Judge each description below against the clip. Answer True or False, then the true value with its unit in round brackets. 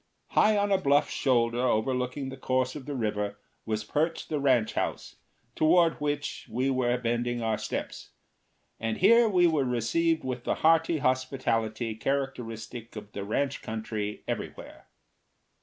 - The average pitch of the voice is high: False (130 Hz)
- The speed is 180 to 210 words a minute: False (145 wpm)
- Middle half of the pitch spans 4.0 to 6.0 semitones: True (4.4 semitones)